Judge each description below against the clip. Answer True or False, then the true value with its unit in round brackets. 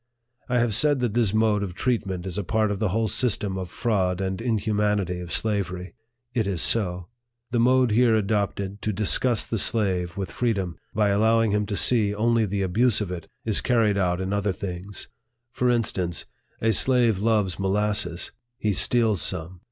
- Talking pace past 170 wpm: True (180 wpm)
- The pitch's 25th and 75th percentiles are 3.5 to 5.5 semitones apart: False (3.1 semitones)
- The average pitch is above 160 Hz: False (105 Hz)